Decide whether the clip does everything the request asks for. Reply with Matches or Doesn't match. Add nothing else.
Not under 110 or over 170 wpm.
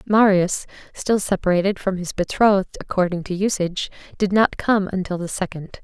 Matches